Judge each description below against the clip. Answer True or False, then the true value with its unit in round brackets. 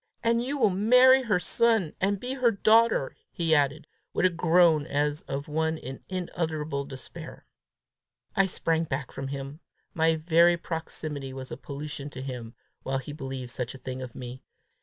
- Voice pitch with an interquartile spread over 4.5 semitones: True (5.2 semitones)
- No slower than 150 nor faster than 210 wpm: True (170 wpm)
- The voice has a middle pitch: True (155 Hz)